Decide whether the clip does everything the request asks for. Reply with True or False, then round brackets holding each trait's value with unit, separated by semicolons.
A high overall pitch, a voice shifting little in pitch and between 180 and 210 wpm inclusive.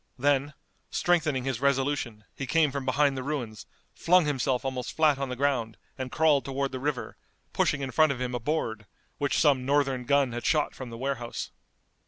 False (135 Hz; 2.3 semitones; 190 wpm)